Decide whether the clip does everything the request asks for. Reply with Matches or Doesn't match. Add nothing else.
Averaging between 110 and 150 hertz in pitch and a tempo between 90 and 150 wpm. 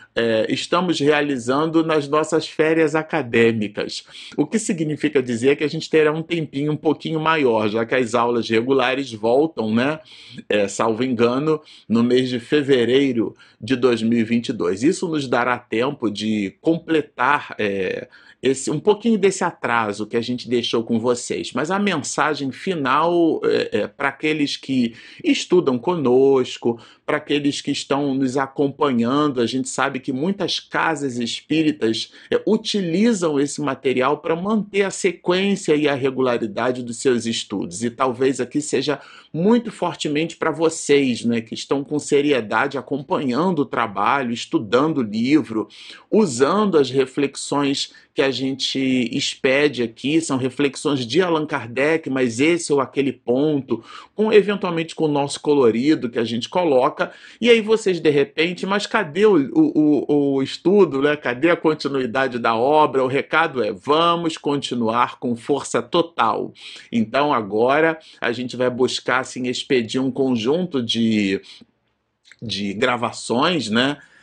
Matches